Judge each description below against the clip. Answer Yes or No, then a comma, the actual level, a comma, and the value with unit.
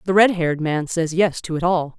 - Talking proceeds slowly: No, fast, 270 wpm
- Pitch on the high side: No, medium, 170 Hz